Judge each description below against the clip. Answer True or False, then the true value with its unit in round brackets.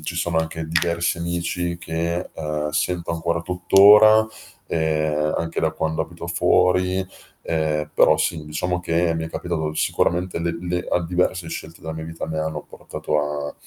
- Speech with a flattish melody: True (1.8 semitones)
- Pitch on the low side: True (85 Hz)